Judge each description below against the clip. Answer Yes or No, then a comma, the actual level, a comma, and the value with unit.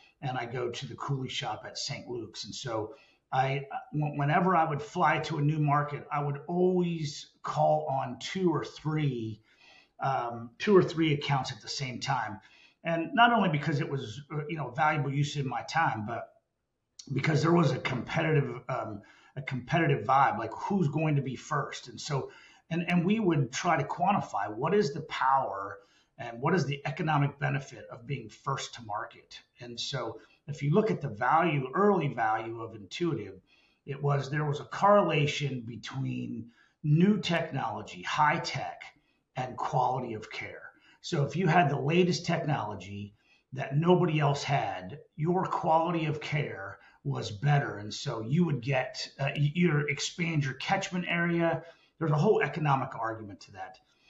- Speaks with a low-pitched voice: No, medium, 150 Hz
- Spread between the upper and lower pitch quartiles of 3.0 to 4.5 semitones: Yes, average, 3.4 semitones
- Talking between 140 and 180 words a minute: Yes, average, 170 wpm